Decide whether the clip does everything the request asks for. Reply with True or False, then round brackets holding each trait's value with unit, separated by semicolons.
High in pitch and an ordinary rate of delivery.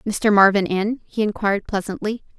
True (205 Hz; 150 wpm)